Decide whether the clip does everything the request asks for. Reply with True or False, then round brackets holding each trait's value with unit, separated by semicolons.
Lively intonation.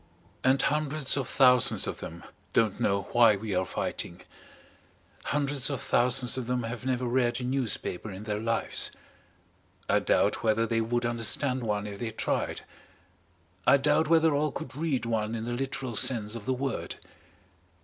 False (3.2 semitones)